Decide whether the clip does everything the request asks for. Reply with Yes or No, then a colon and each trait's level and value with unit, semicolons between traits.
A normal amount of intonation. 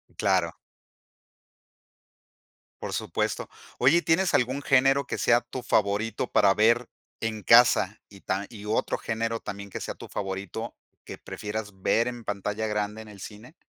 Yes: average, 3.1 semitones